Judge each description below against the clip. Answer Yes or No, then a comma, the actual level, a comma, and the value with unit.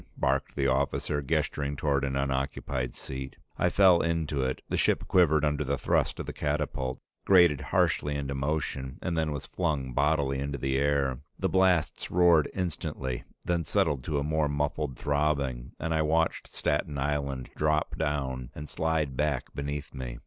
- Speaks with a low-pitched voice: Yes, very low, 70 Hz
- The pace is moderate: Yes, average, 165 wpm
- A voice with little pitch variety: Yes, narrow, 2.3 semitones